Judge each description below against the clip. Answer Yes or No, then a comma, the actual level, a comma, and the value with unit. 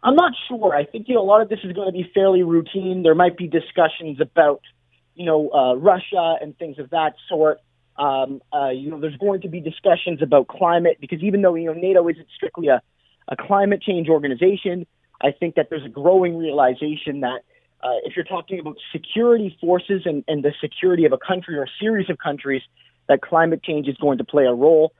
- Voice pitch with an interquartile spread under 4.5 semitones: Yes, average, 3.9 semitones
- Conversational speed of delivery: No, fast, 220 wpm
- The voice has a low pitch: No, medium, 165 Hz